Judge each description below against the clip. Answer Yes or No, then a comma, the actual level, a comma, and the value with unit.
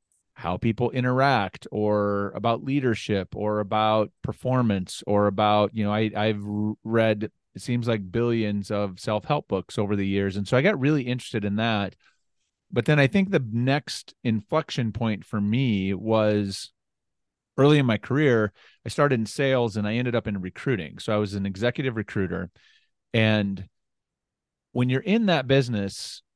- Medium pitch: No, low, 110 Hz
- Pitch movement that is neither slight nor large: Yes, average, 3.4 semitones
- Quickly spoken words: No, average, 165 wpm